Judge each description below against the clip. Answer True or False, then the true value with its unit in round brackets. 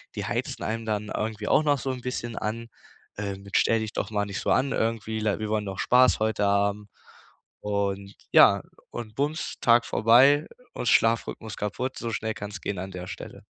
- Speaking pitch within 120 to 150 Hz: False (110 Hz)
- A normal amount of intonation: False (2.3 semitones)